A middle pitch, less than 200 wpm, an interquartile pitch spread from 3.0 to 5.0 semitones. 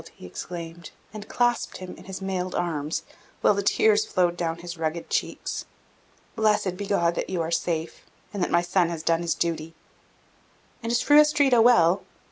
Yes: medium, 175 Hz; average, 180 wpm; average, 3.6 semitones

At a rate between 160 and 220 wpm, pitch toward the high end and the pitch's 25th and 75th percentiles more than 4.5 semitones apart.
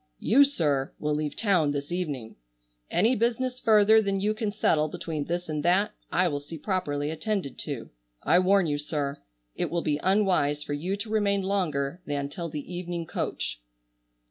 No: average, 175 wpm; medium, 175 Hz; wide, 5.4 semitones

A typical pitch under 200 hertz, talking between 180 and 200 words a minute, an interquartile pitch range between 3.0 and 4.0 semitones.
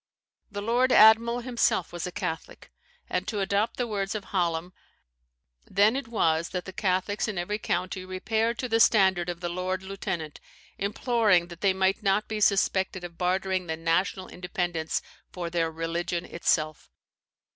No: high, 190 Hz; average, 160 wpm; average, 3.4 semitones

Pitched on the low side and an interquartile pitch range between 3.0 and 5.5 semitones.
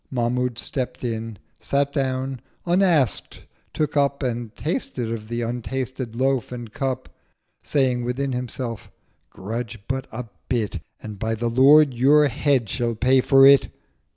No: low, 125 Hz; narrow, 2.6 semitones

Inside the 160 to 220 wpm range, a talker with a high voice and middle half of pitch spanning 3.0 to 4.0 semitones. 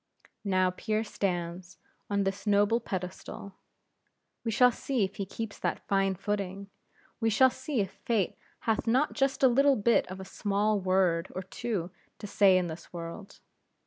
Yes: average, 165 wpm; high, 200 Hz; average, 3.3 semitones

